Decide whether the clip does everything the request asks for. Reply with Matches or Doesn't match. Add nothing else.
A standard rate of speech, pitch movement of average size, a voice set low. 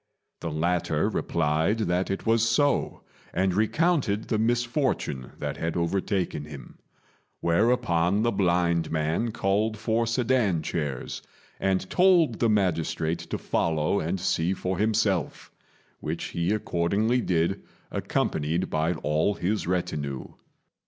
Doesn't match